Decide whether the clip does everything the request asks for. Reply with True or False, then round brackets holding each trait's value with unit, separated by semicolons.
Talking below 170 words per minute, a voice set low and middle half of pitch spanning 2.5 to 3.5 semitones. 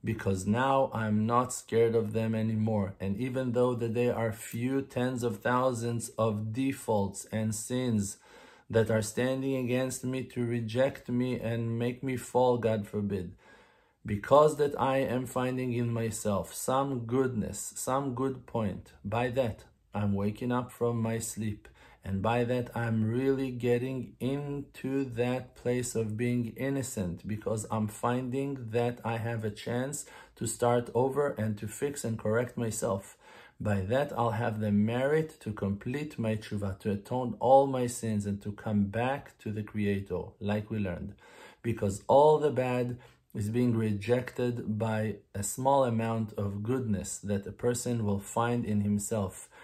True (155 wpm; 115 Hz; 2.9 semitones)